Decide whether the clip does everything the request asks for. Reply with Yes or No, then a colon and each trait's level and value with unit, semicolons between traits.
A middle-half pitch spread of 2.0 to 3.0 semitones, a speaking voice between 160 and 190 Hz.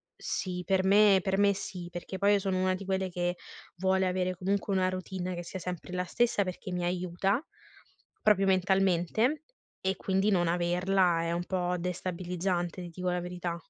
No: narrow, 1.5 semitones; medium, 185 Hz